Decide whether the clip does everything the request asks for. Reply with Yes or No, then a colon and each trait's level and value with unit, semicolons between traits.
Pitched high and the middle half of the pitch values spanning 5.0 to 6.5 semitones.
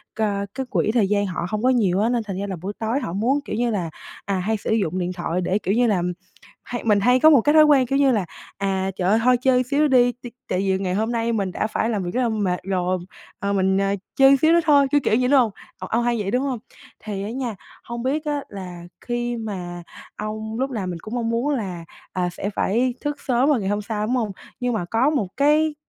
No: high, 220 Hz; average, 4.3 semitones